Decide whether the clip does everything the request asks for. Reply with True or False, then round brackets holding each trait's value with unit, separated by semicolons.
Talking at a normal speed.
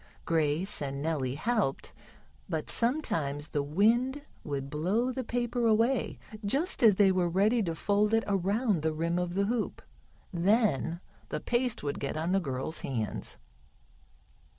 True (150 wpm)